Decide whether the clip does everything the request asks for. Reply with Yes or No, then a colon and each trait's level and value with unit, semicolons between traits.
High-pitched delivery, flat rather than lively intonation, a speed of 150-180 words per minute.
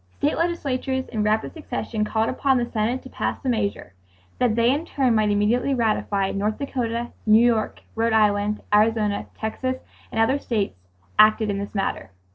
No: high, 225 Hz; average, 3.2 semitones; average, 170 wpm